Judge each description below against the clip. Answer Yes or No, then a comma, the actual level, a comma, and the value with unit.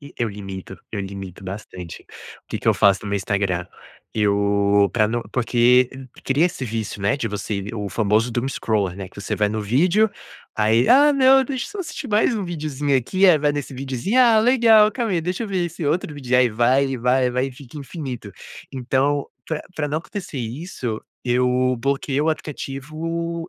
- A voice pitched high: No, low, 130 Hz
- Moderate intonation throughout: No, wide, 7.5 semitones